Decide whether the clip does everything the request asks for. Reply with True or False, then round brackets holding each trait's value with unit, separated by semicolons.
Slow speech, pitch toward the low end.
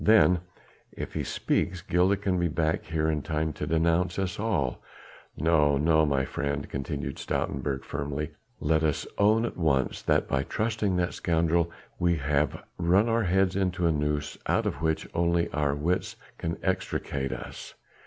False (165 wpm; 80 Hz)